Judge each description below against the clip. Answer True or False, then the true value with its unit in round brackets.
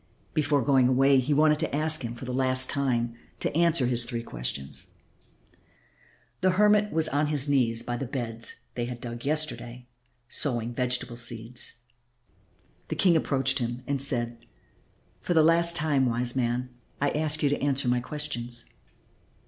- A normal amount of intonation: True (3.8 semitones)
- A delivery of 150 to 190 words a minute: True (160 wpm)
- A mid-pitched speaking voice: False (130 Hz)